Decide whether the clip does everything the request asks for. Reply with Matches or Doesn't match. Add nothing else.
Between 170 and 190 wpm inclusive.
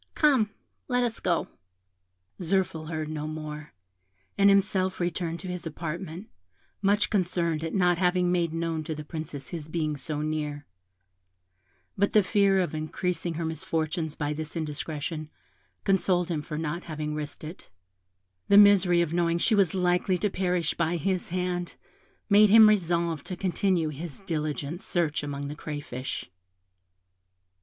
Doesn't match